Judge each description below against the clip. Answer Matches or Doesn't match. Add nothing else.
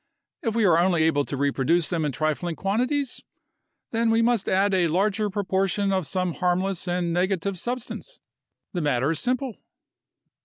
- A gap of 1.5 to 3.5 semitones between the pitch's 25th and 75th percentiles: Doesn't match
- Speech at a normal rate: Matches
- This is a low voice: Doesn't match